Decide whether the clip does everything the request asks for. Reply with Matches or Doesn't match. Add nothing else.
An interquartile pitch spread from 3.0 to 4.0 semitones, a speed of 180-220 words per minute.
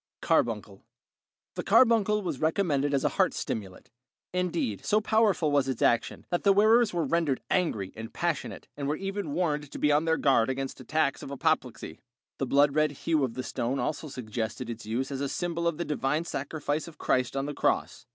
Doesn't match